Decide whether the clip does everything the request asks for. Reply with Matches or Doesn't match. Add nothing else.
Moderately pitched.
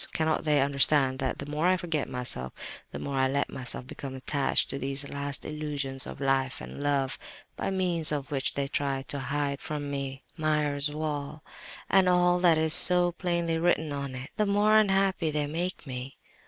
Matches